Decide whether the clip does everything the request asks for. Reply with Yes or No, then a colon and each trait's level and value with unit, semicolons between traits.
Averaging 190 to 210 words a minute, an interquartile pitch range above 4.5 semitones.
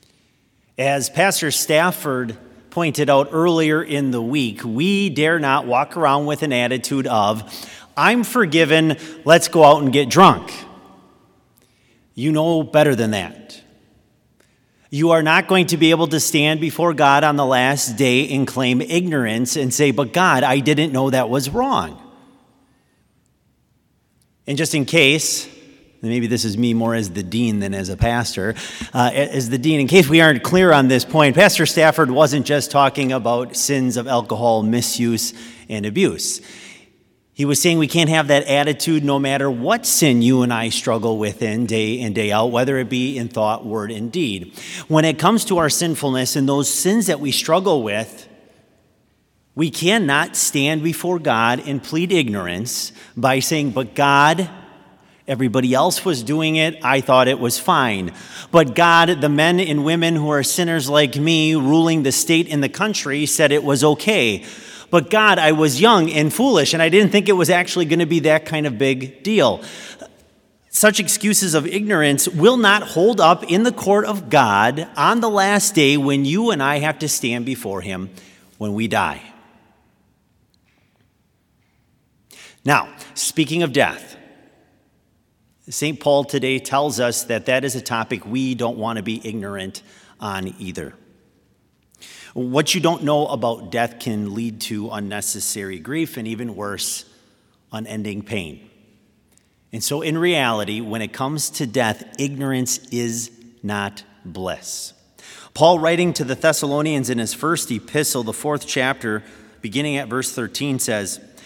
No: average, 165 wpm; average, 5.2 semitones